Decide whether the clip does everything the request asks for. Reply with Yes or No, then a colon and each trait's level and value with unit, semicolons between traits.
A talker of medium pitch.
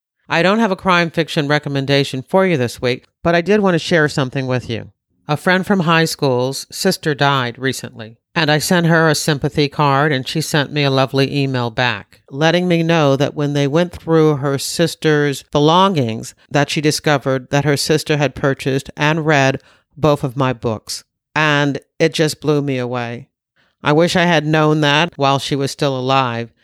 Yes: medium, 145 Hz